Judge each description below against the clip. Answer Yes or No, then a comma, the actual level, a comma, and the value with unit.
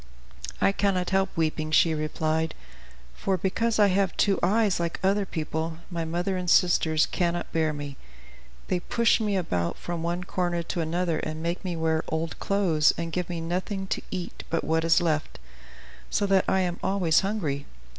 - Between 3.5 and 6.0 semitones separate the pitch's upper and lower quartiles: No, average, 3.0 semitones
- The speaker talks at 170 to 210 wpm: Yes, average, 180 wpm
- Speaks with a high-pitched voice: No, medium, 175 Hz